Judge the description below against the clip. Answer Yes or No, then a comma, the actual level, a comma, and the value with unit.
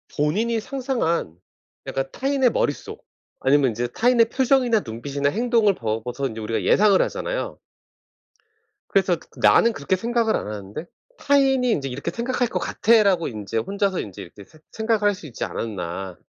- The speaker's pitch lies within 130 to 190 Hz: Yes, medium, 185 Hz